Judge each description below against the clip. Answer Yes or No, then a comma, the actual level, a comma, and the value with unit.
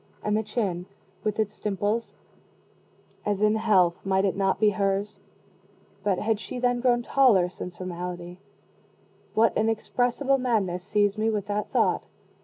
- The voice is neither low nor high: No, high, 210 Hz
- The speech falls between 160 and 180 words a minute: No, average, 150 wpm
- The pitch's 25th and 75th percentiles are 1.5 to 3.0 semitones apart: Yes, narrow, 2.6 semitones